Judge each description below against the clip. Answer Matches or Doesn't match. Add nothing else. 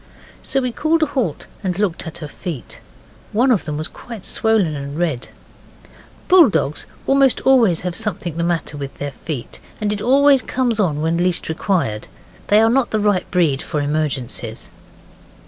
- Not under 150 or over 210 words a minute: Matches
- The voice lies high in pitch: Doesn't match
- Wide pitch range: Matches